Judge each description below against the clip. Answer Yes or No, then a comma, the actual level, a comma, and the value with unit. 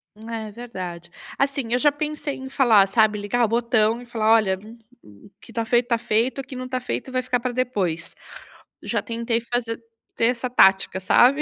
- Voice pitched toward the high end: Yes, high, 235 Hz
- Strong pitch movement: No, average, 2.8 semitones